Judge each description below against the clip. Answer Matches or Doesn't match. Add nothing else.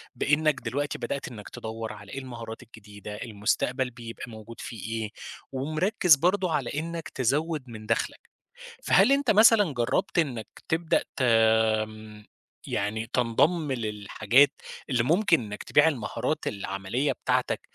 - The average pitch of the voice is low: Matches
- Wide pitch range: Matches